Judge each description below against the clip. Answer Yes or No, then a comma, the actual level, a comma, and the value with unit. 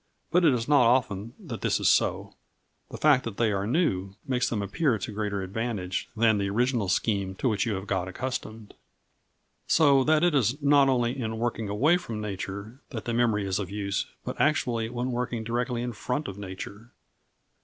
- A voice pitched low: Yes, low, 115 Hz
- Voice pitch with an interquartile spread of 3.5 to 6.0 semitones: Yes, average, 4.0 semitones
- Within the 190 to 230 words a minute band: Yes, average, 195 wpm